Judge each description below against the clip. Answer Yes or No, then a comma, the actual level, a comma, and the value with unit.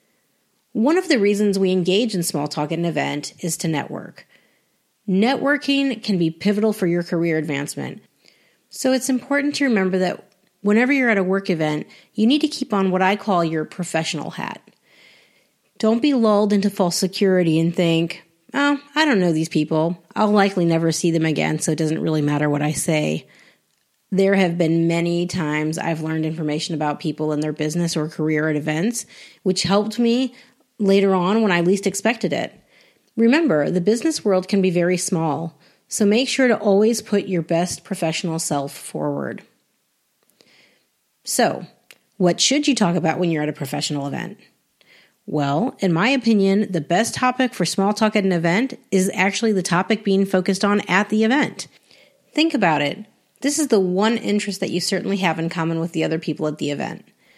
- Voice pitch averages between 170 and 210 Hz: Yes, medium, 185 Hz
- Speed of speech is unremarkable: Yes, average, 185 wpm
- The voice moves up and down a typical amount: Yes, average, 4.9 semitones